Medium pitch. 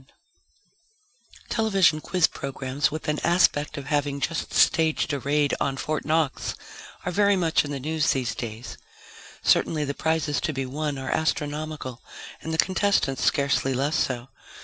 Yes: medium, 150 Hz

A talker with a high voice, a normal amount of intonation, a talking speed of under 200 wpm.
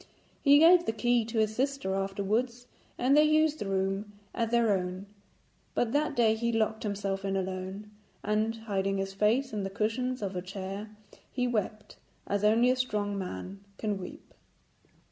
Yes: high, 215 Hz; average, 3.7 semitones; average, 170 wpm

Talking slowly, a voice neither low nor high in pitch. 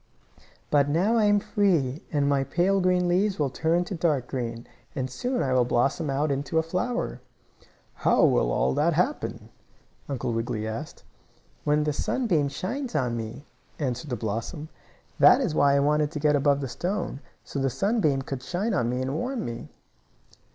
No: average, 180 wpm; medium, 145 Hz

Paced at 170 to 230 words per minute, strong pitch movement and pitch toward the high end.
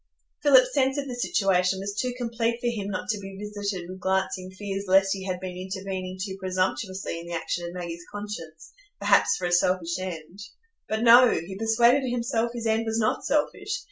No: average, 190 wpm; average, 3.8 semitones; high, 195 Hz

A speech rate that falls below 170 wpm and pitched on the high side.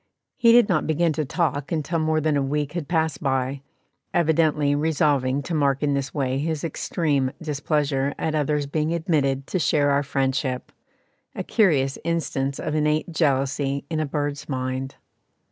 No: average, 160 wpm; medium, 145 Hz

